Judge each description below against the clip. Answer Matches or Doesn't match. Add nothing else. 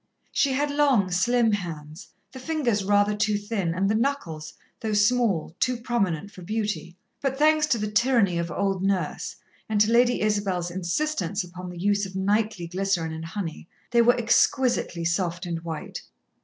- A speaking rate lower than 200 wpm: Matches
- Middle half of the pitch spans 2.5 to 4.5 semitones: Doesn't match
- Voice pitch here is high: Matches